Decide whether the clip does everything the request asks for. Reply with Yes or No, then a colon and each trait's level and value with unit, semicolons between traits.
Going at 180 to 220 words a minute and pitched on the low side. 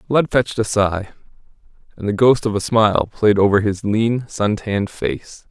Yes: average, 185 wpm; low, 105 Hz